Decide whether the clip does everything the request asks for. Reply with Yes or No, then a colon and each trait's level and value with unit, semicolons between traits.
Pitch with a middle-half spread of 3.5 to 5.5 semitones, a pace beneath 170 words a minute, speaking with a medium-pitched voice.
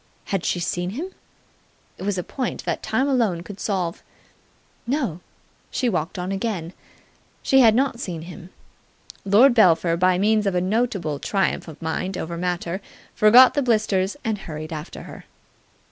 No: average, 4.5 semitones; average, 160 wpm; high, 195 Hz